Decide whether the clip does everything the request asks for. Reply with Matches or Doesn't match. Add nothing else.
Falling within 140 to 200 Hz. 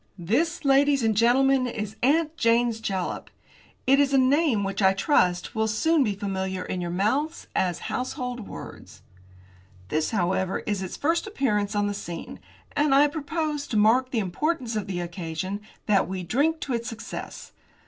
Doesn't match